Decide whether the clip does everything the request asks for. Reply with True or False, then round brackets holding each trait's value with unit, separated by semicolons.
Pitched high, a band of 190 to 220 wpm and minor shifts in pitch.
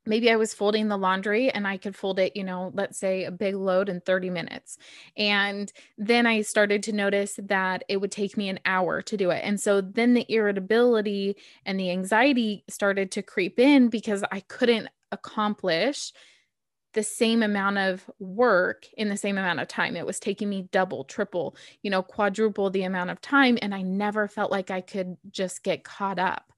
True (200 Hz; 200 wpm; 2.2 semitones)